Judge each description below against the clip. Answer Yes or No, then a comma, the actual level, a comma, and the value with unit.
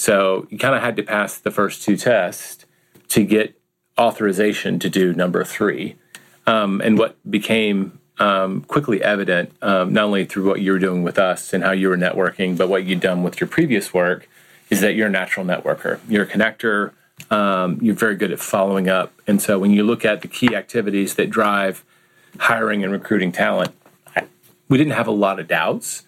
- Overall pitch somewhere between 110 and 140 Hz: No, low, 100 Hz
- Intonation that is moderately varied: No, narrow, 1.9 semitones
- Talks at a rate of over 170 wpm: Yes, average, 200 wpm